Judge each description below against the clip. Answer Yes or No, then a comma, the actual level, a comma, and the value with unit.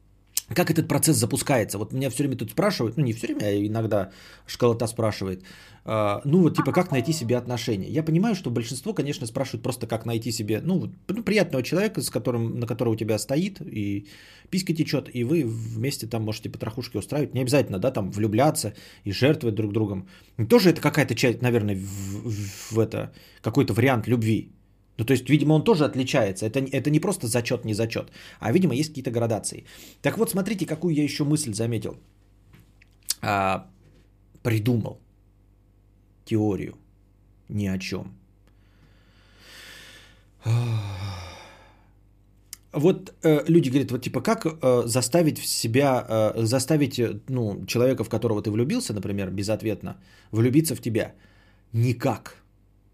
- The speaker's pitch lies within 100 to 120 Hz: Yes, low, 115 Hz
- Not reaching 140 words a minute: No, average, 155 wpm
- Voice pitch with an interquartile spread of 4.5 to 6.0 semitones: Yes, average, 5.1 semitones